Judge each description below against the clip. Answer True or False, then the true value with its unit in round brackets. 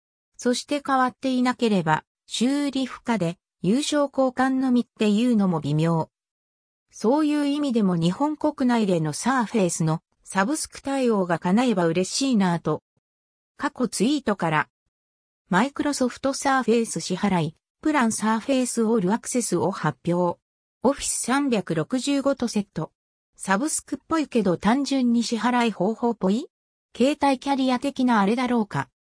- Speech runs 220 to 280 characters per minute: False (315 characters per minute)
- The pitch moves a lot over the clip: True (6.8 semitones)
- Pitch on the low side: False (235 Hz)